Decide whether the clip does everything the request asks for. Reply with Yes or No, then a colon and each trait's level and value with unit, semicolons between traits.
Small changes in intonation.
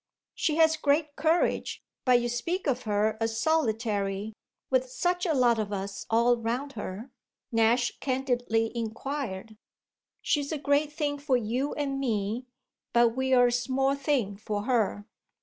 No: average, 4.1 semitones